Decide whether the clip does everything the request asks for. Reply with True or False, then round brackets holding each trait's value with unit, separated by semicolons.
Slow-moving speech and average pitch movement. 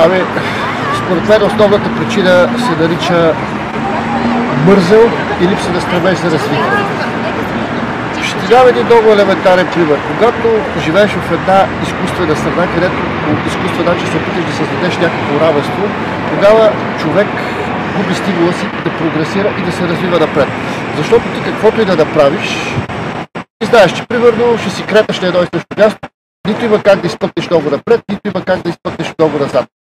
False (165 wpm; 3.9 semitones)